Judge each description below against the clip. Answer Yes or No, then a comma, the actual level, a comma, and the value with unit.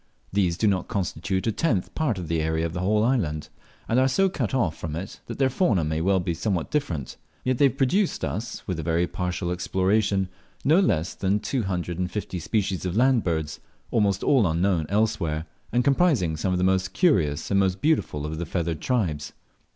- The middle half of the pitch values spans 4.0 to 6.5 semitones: Yes, average, 5.3 semitones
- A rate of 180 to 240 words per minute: Yes, fast, 205 wpm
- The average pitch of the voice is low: Yes, very low, 95 Hz